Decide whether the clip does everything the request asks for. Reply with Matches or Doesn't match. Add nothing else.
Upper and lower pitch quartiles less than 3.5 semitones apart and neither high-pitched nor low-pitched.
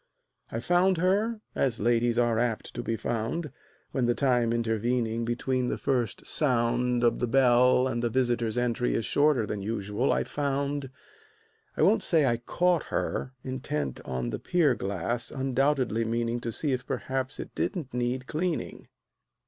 Doesn't match